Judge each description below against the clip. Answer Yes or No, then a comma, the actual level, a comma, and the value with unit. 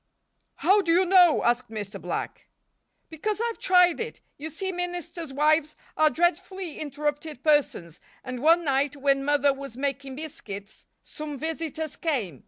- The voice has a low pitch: No, very high, 300 Hz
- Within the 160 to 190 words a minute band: No, average, 145 wpm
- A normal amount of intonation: Yes, average, 4.1 semitones